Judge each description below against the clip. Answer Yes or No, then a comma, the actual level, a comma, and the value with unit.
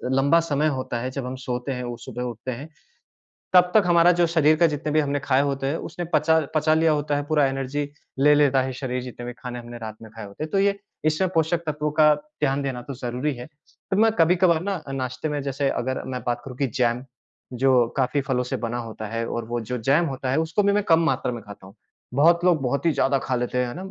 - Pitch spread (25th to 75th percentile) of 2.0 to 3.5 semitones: No, average, 3.9 semitones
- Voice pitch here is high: No, low, 135 Hz